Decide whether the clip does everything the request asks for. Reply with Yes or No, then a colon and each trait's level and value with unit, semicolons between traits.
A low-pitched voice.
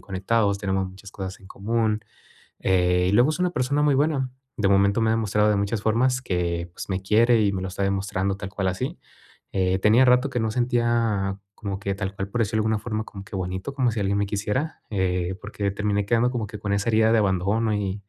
Yes: low, 105 Hz